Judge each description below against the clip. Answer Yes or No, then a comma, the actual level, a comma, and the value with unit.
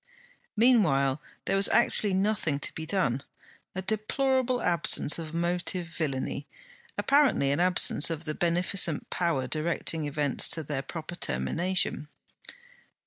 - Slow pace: Yes, slow, 125 wpm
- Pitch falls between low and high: Yes, medium, 170 Hz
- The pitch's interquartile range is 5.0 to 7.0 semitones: No, average, 4.2 semitones